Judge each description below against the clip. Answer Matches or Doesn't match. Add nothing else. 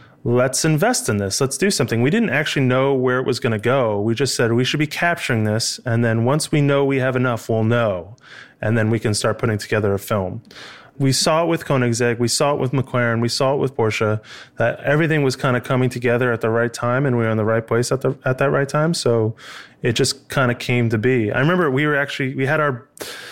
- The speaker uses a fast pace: Matches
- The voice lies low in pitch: Matches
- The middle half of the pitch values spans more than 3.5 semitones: Doesn't match